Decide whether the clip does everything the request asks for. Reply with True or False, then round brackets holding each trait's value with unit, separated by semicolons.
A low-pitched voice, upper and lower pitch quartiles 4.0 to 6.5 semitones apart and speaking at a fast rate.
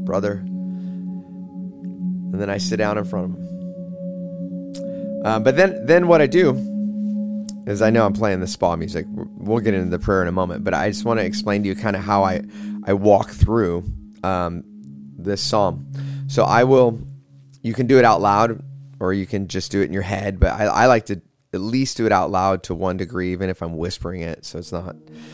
True (100 Hz; 5.1 semitones; 215 wpm)